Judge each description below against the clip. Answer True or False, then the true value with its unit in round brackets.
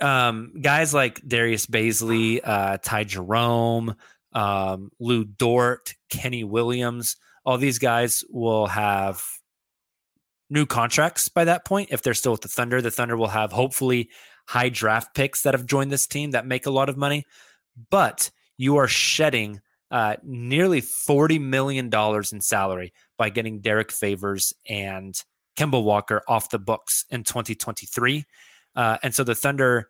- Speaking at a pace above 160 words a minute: False (150 wpm)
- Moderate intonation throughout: True (3.6 semitones)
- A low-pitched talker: True (120 Hz)